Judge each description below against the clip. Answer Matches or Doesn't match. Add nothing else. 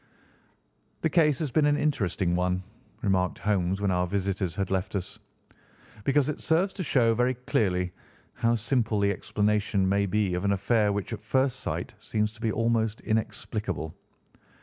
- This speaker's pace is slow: Doesn't match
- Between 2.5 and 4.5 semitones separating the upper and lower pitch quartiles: Matches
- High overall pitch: Doesn't match